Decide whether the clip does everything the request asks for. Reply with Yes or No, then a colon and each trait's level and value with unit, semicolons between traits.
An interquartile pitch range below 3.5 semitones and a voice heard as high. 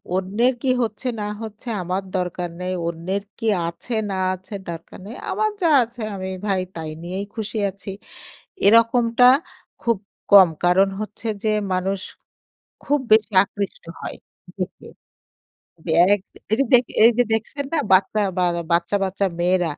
No: average, 3.8 semitones; high, 200 Hz